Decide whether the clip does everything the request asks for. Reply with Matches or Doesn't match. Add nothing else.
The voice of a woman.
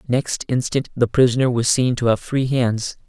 Doesn't match